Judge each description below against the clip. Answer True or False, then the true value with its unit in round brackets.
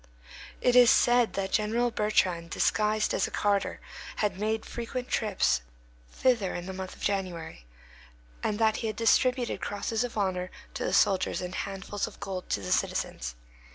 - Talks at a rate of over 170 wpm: False (165 wpm)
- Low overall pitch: False (205 Hz)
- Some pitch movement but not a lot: True (3.4 semitones)